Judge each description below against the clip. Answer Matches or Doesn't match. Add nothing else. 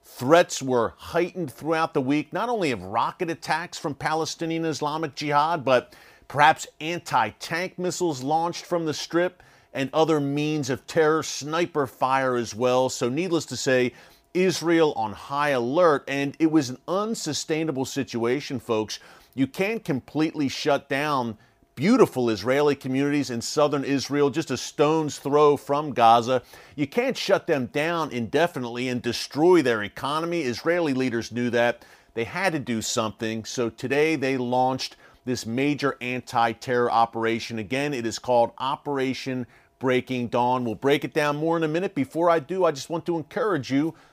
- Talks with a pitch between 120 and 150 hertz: Matches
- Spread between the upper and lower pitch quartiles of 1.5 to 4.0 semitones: Doesn't match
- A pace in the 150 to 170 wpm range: Matches